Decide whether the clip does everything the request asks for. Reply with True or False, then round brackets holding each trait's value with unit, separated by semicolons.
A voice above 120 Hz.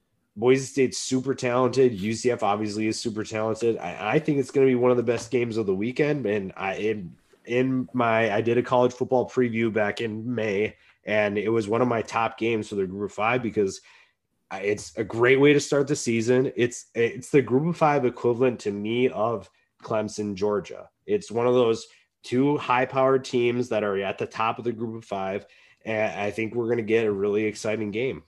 False (115 Hz)